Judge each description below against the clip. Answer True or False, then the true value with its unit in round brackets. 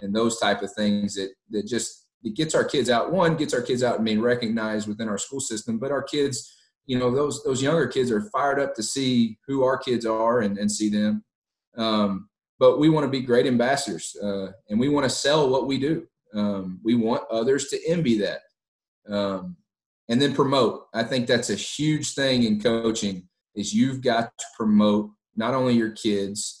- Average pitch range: True (4.1 semitones)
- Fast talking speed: True (210 wpm)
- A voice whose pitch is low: True (115 Hz)